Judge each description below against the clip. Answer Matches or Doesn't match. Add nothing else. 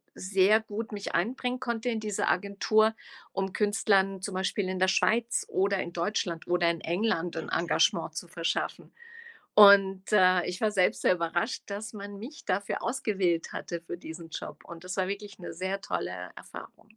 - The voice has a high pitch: Matches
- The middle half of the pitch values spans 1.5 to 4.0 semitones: Matches